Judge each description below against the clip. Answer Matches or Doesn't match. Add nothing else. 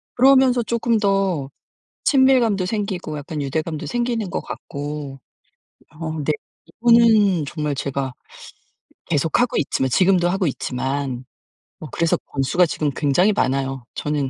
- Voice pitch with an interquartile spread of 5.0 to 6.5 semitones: Doesn't match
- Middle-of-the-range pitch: Matches